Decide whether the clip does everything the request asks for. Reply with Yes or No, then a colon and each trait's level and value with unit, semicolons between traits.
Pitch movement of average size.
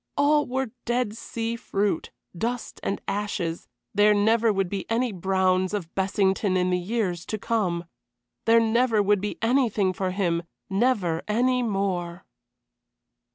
Yes: average, 3.7 semitones